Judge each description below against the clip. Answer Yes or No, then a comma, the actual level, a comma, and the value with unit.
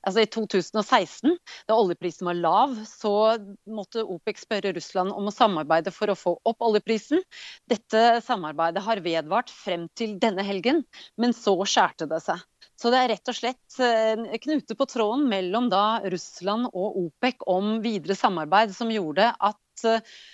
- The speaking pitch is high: Yes, high, 220 Hz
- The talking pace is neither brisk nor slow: Yes, average, 155 wpm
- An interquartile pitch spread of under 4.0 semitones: Yes, average, 3.5 semitones